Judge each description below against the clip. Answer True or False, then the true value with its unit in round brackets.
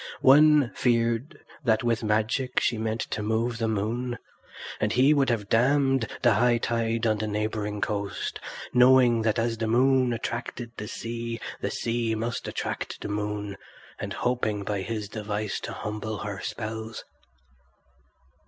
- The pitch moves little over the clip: True (2.1 semitones)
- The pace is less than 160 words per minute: True (150 wpm)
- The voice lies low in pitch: True (115 Hz)